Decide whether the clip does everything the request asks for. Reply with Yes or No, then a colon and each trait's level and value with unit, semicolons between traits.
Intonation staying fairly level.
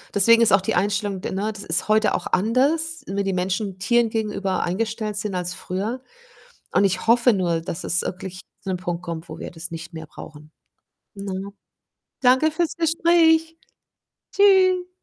No: average, 5.0 semitones